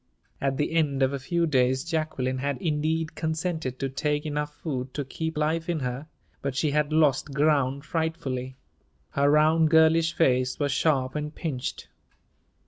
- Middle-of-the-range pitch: Yes, medium, 150 Hz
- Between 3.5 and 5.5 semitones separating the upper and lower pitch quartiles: No, average, 3.1 semitones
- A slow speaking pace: No, average, 160 wpm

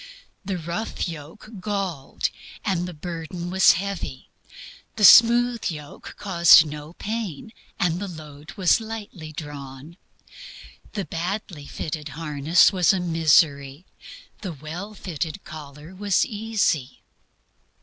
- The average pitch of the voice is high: No, medium, 170 Hz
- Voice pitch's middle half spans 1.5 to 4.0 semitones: No, average, 4.6 semitones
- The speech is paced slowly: Yes, slow, 115 wpm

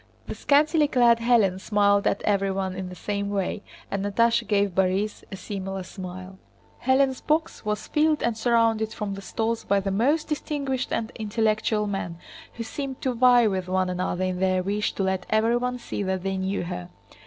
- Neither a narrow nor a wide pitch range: Yes, average, 3.7 semitones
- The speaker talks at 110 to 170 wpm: No, average, 180 wpm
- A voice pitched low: No, high, 205 Hz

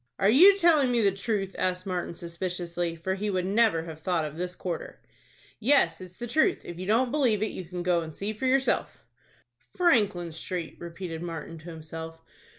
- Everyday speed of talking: Yes, average, 190 wpm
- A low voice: No, medium, 185 Hz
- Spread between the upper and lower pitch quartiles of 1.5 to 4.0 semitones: No, average, 4.5 semitones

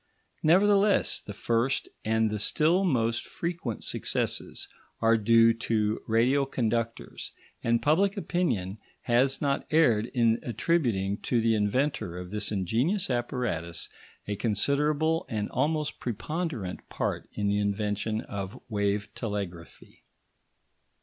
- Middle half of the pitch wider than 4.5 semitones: Yes, wide, 5.6 semitones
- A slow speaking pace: Yes, slow, 115 wpm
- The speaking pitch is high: No, low, 115 Hz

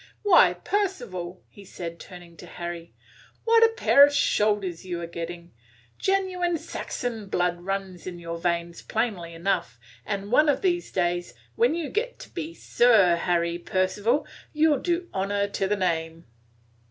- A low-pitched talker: No, high, 195 Hz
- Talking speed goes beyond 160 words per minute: No, average, 155 wpm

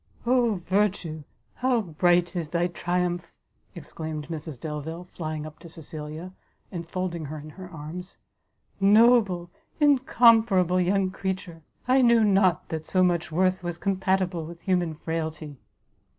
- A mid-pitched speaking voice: Yes, medium, 175 Hz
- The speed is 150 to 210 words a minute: No, slow, 135 wpm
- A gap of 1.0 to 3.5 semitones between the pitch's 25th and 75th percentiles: Yes, average, 3.0 semitones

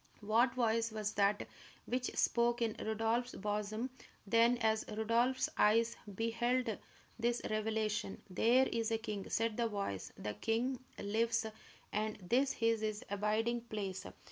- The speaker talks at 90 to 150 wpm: Yes, slow, 135 wpm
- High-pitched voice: Yes, high, 225 Hz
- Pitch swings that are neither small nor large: No, narrow, 1.9 semitones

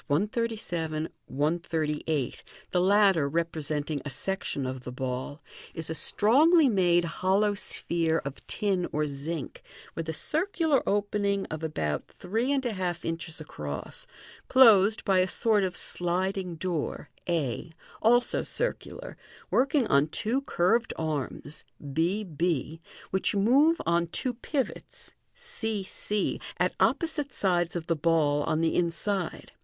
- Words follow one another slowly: Yes, slow, 130 wpm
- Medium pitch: Yes, medium, 175 Hz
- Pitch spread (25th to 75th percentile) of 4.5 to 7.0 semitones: Yes, average, 5.1 semitones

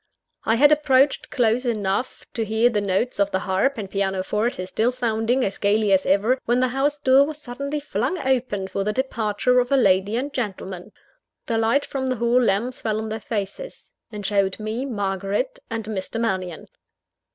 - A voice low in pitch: No, high, 225 Hz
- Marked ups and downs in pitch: No, average, 4.2 semitones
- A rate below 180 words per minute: No, average, 185 wpm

